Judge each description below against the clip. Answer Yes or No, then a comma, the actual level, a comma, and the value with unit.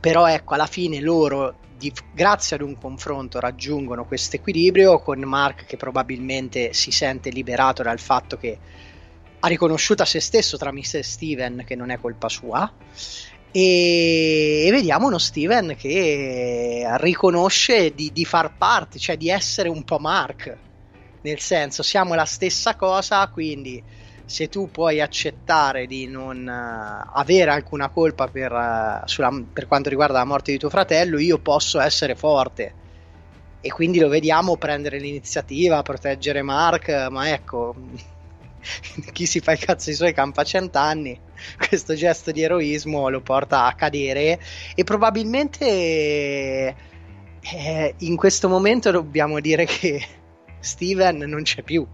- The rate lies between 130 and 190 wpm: Yes, average, 145 wpm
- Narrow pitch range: No, average, 4.7 semitones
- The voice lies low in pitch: No, medium, 145 Hz